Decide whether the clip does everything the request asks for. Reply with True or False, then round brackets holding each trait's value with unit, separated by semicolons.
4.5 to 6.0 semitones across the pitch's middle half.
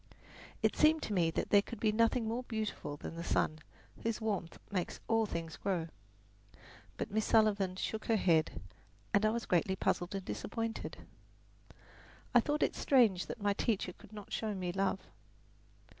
False (3.7 semitones)